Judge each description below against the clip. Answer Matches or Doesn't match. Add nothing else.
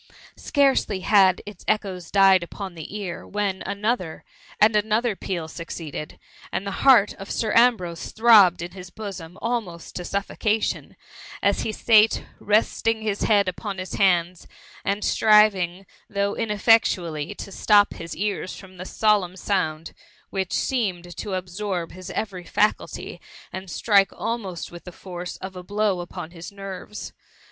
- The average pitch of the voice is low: Doesn't match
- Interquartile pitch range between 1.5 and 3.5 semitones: Matches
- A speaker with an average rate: Matches